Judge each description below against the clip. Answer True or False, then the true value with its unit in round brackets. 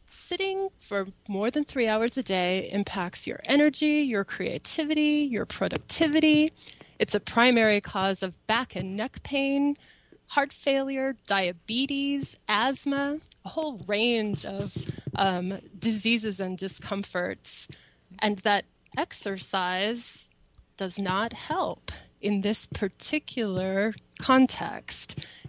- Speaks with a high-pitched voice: True (220 Hz)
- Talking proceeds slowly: True (110 wpm)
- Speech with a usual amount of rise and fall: False (6.1 semitones)